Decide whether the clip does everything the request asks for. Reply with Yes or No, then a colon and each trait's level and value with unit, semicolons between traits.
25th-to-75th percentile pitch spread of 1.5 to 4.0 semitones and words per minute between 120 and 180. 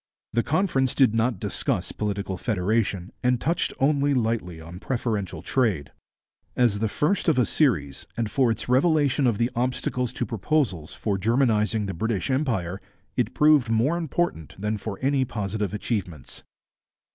No: average, 4.8 semitones; average, 150 wpm